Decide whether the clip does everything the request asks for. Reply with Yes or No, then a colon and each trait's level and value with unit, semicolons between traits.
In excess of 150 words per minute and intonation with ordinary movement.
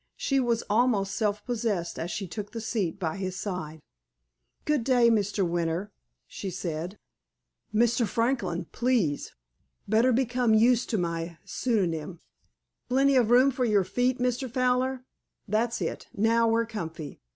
No: average, 140 wpm; average, 5.0 semitones